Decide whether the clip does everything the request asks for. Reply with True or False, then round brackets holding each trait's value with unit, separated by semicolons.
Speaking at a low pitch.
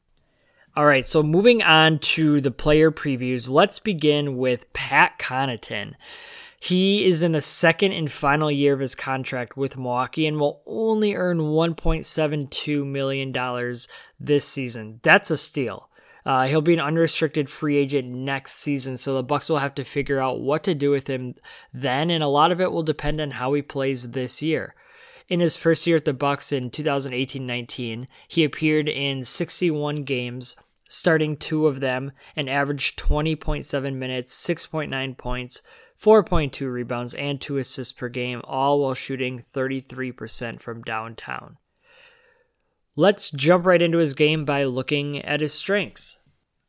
False (145 Hz)